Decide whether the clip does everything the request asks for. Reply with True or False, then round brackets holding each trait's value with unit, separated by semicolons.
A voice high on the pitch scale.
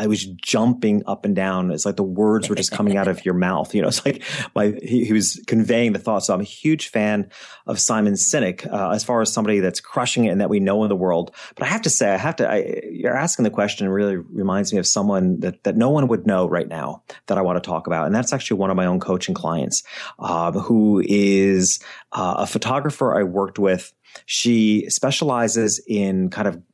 False (100 Hz)